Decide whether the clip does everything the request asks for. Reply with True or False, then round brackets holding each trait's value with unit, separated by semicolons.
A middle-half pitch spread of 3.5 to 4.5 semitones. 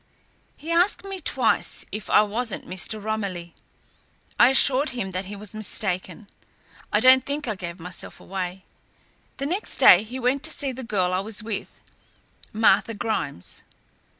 False (5.4 semitones)